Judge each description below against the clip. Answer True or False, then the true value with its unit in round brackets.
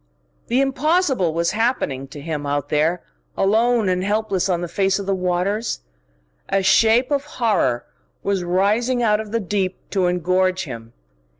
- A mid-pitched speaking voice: False (195 Hz)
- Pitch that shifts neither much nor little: True (4.3 semitones)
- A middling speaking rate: True (160 wpm)